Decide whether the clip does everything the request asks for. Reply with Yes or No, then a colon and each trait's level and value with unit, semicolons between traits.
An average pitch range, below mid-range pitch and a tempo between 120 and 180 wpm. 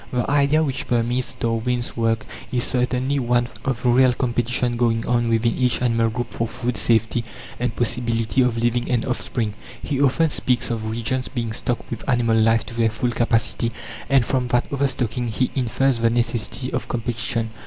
No: narrow, 1.6 semitones; low, 120 Hz; average, 175 wpm